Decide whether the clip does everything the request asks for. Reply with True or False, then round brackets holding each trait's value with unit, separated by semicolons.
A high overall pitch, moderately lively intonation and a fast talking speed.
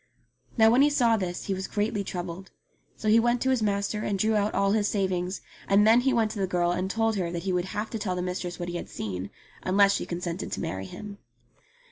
True (200 Hz; 3.3 semitones; 245 wpm)